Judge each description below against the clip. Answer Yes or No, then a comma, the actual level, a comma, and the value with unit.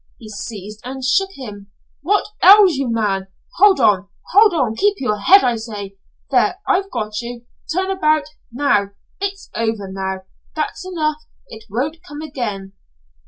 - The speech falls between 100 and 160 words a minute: Yes, average, 155 wpm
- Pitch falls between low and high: No, very high, 255 Hz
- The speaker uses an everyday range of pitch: No, wide, 9.0 semitones